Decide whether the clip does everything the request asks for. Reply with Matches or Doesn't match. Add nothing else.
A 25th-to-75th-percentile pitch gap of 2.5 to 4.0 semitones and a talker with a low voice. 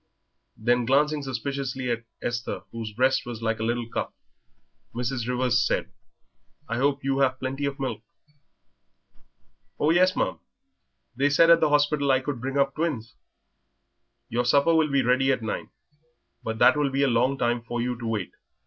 Matches